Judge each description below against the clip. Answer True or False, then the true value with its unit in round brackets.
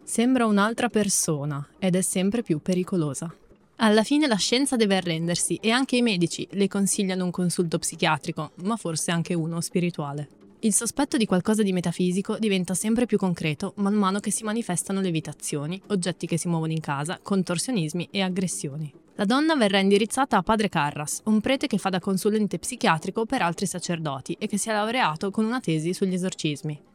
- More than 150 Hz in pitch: True (190 Hz)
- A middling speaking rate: False (180 wpm)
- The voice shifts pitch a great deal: False (4.3 semitones)